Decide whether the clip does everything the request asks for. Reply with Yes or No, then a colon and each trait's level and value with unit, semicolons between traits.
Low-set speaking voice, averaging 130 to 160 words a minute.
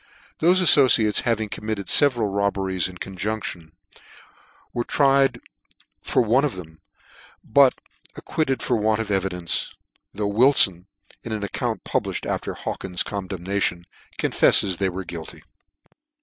Yes: low, 105 Hz; average, 145 wpm